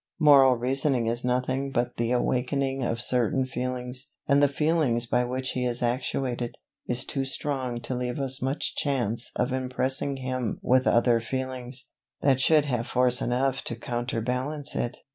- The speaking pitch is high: No, low, 130 Hz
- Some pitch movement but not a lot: No, narrow, 1.7 semitones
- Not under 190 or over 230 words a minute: No, average, 160 wpm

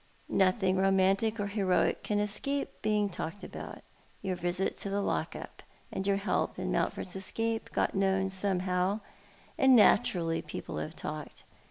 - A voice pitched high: Yes, high, 195 Hz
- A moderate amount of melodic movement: No, narrow, 1.9 semitones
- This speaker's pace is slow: No, average, 155 wpm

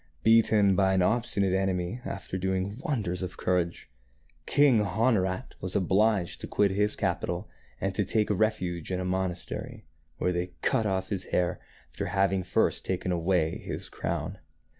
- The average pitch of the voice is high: No, very low, 95 Hz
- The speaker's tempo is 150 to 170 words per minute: Yes, average, 155 wpm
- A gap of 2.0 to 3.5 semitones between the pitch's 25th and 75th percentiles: Yes, narrow, 2.4 semitones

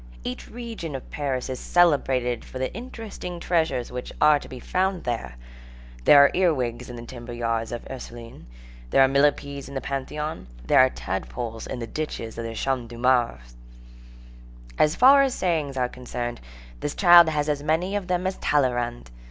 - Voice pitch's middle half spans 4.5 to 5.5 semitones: Yes, average, 5.1 semitones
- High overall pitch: No, low, 135 Hz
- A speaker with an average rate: Yes, average, 185 wpm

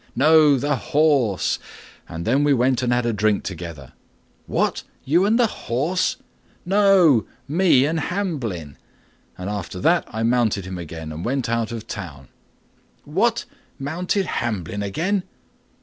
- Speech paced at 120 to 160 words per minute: Yes, average, 140 wpm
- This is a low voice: Yes, low, 125 Hz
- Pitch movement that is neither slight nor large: No, wide, 8.0 semitones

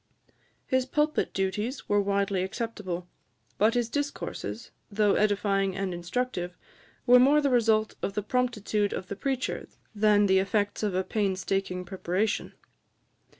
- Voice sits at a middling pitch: No, high, 205 Hz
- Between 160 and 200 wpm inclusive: No, slow, 135 wpm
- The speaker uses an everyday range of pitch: Yes, average, 3.6 semitones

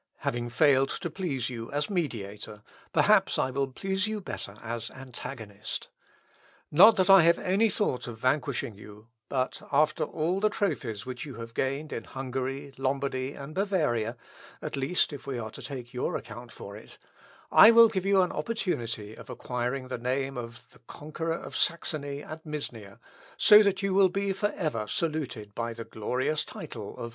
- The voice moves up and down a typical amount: No, wide, 6.3 semitones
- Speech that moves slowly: No, average, 175 wpm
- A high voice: No, low, 135 Hz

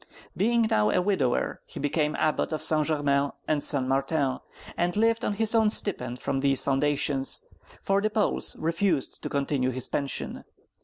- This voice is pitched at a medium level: Yes, medium, 150 Hz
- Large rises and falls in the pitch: Yes, wide, 6.2 semitones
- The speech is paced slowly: No, average, 160 wpm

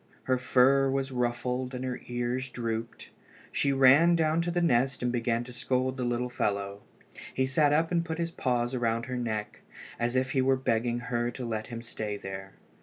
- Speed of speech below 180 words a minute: No, average, 195 wpm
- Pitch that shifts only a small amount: Yes, narrow, 2.0 semitones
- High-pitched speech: No, low, 125 Hz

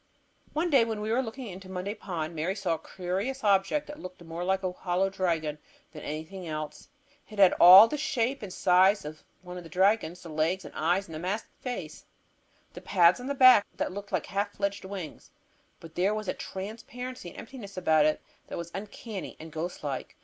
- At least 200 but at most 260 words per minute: Yes, fast, 205 wpm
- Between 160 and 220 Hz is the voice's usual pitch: Yes, high, 190 Hz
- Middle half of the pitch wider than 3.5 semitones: Yes, average, 3.9 semitones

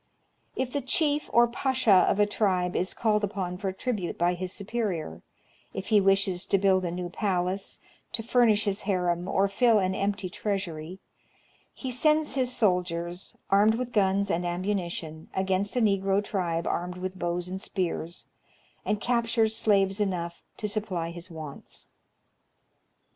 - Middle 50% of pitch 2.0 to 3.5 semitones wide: Yes, average, 3.2 semitones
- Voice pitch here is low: No, high, 195 Hz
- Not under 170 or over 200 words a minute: No, average, 155 wpm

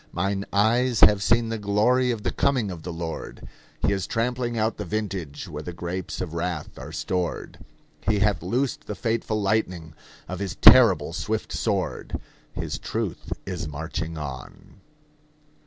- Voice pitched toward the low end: Yes, low, 100 Hz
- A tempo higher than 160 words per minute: No, average, 155 wpm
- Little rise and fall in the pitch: No, average, 4.8 semitones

